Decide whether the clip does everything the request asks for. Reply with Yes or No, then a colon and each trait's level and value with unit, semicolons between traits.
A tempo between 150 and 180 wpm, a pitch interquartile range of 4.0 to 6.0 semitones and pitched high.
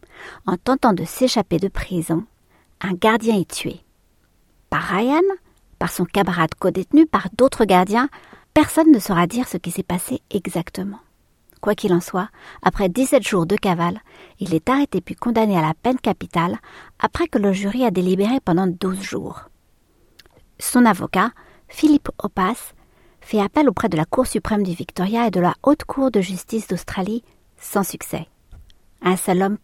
Yes: average, 165 wpm; average, 5.1 semitones; high, 200 Hz